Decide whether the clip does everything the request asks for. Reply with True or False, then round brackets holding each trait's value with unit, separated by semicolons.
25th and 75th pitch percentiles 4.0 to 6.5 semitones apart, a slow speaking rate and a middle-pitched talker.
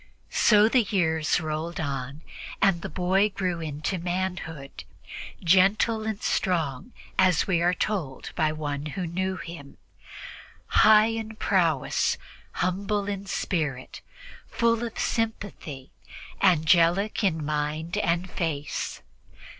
True (4.3 semitones; 115 wpm; 175 Hz)